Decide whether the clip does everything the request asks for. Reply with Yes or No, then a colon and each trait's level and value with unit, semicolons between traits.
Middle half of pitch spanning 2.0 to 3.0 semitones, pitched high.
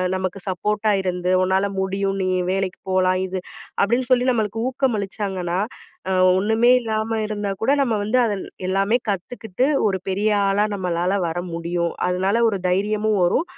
Yes: average, 2.7 semitones; high, 195 Hz